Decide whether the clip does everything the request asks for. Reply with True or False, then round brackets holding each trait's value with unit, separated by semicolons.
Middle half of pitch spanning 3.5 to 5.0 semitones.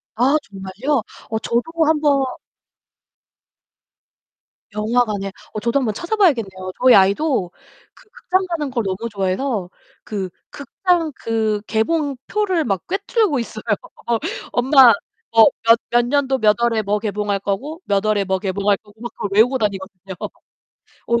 False (5.6 semitones)